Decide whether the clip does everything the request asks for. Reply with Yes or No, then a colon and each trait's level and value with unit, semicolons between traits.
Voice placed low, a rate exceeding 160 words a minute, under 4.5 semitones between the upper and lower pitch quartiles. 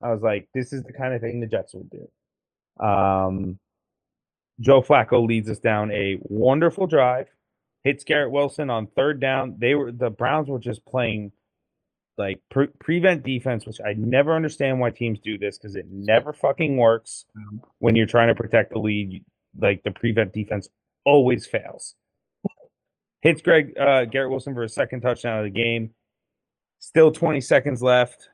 Yes: low, 120 Hz; average, 170 wpm; average, 4.0 semitones